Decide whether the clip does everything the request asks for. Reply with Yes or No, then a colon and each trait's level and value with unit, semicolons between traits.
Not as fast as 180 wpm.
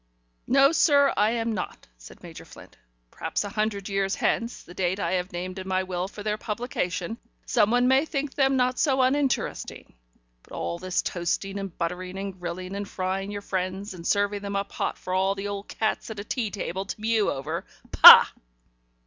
No: average, 190 wpm